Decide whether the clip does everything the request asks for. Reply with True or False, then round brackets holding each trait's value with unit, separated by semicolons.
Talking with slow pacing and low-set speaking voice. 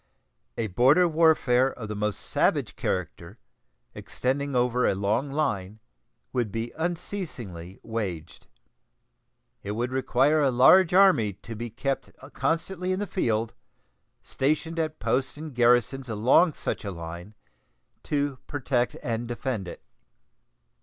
True (125 wpm; 125 Hz)